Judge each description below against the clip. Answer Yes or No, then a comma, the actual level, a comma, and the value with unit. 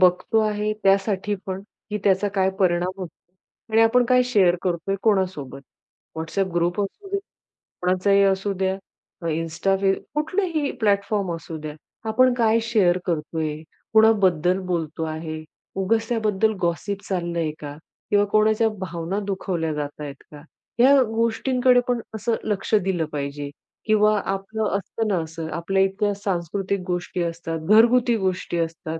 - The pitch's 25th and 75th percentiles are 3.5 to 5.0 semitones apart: Yes, average, 4.2 semitones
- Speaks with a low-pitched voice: No, high, 195 Hz